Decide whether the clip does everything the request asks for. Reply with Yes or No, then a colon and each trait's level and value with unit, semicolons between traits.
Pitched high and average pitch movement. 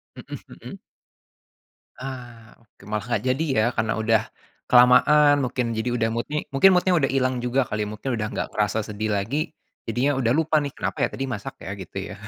No: low, 120 Hz; average, 3.7 semitones